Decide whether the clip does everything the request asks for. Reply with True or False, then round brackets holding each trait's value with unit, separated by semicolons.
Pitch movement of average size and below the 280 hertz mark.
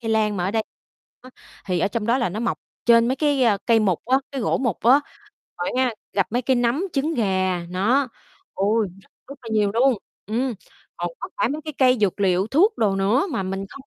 True (4.8 semitones; 230 Hz)